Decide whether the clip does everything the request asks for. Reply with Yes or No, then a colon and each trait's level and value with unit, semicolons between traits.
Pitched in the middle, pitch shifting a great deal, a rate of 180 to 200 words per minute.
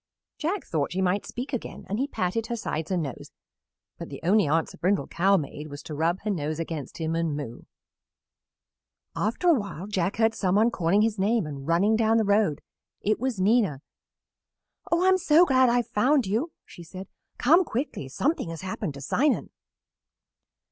No: high, 200 Hz; wide, 6.2 semitones; average, 190 wpm